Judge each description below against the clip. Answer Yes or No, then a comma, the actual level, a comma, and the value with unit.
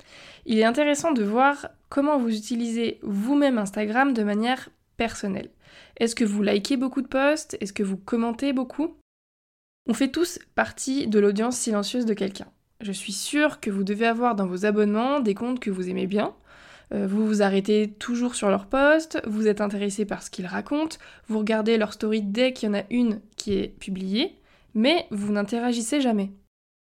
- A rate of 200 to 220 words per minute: No, average, 180 wpm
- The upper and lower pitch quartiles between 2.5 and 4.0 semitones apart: No, average, 4.4 semitones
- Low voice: No, high, 225 Hz